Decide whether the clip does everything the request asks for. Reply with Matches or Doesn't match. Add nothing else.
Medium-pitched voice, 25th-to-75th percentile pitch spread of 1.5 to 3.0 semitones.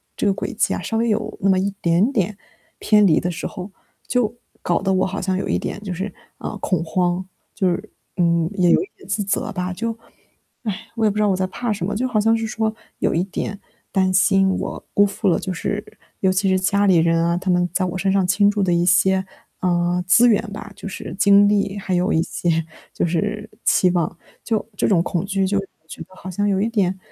Doesn't match